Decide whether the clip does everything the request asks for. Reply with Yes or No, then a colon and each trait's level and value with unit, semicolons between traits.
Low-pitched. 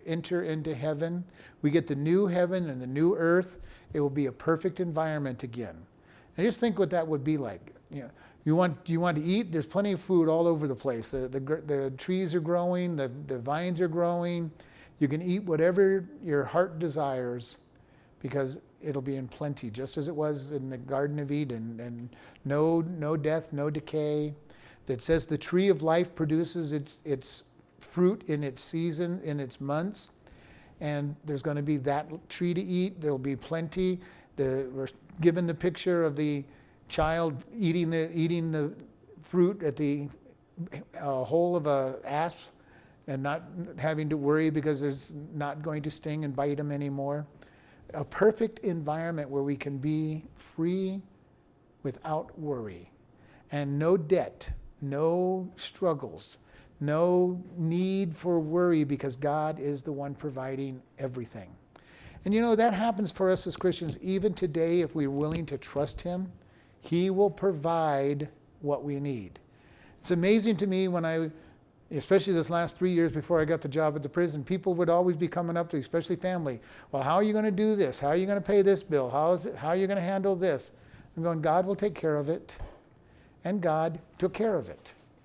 No: medium, 160 Hz